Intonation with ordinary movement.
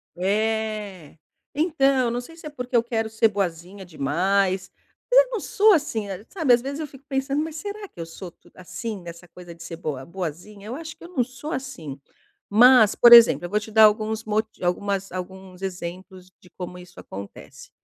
No: wide, 6.2 semitones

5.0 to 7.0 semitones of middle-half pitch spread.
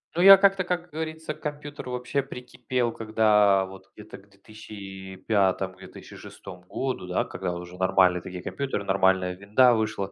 Yes: wide, 5.4 semitones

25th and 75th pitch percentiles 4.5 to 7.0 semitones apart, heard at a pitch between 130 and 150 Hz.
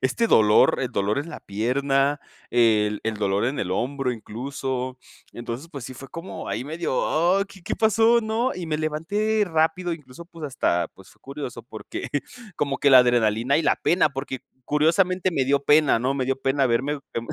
Yes: average, 5.2 semitones; medium, 140 Hz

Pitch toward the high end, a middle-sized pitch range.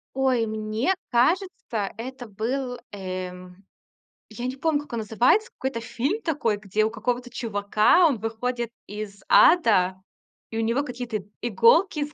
Yes: high, 235 Hz; average, 3.8 semitones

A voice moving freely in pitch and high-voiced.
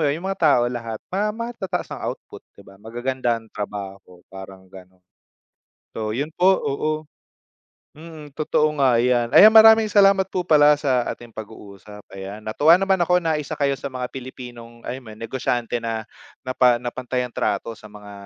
No: wide, 5.9 semitones; low, 125 Hz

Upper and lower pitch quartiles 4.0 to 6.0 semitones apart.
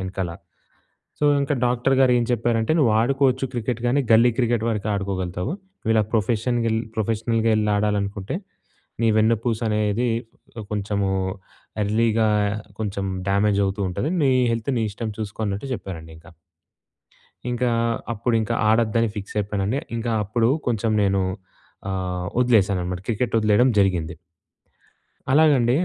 No: average, 3.1 semitones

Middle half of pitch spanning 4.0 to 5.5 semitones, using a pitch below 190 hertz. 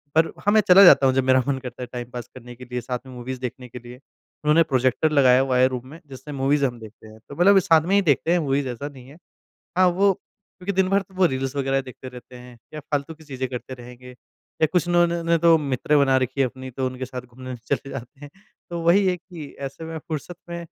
Yes: average, 4.5 semitones; low, 135 Hz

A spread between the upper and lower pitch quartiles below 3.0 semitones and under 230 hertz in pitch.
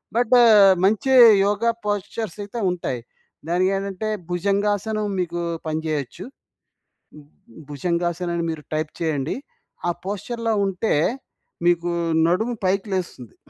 No: average, 3.6 semitones; medium, 185 Hz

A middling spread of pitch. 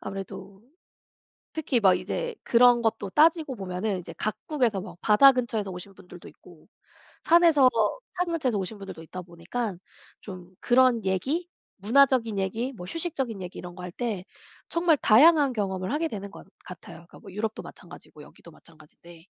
No: wide, 6.1 semitones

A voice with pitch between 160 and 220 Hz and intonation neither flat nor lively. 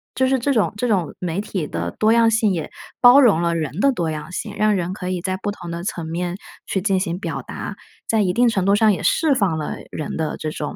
Yes: high, 190 Hz; average, 4.4 semitones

